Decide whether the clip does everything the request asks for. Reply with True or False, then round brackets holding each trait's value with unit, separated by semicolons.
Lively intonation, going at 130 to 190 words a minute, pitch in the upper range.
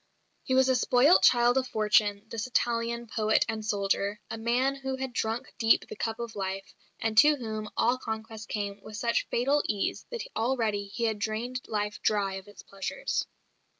False (2.8 semitones; 185 wpm; 225 Hz)